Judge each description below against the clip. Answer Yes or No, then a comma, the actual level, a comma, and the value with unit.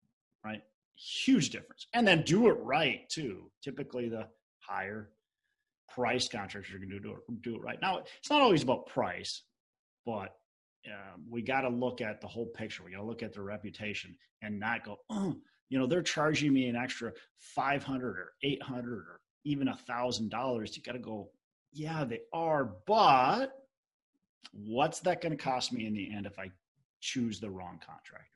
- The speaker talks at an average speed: Yes, average, 185 wpm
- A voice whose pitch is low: Yes, low, 120 Hz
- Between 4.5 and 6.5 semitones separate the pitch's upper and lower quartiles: Yes, average, 5.0 semitones